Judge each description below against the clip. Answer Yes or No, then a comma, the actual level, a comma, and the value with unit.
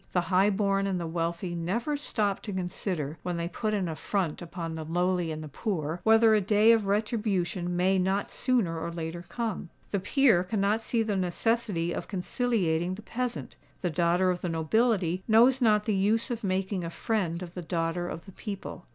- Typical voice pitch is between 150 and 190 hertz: Yes, medium, 185 Hz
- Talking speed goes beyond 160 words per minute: Yes, average, 195 wpm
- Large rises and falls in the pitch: No, average, 3.9 semitones